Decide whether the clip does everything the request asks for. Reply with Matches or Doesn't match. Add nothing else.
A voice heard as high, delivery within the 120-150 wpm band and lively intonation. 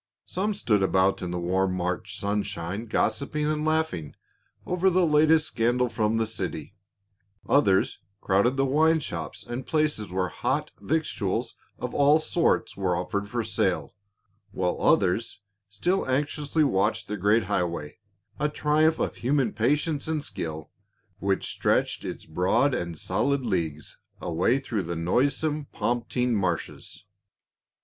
Doesn't match